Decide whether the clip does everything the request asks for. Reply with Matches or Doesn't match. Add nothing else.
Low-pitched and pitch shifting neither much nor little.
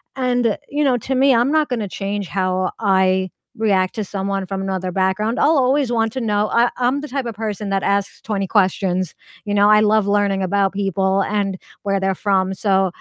Doesn't match